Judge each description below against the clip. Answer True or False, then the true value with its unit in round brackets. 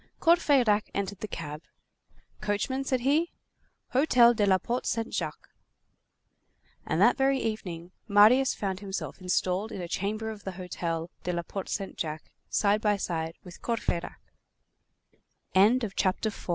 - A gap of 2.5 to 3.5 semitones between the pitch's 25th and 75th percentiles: False (4.6 semitones)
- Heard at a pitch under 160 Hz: False (205 Hz)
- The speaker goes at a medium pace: False (130 wpm)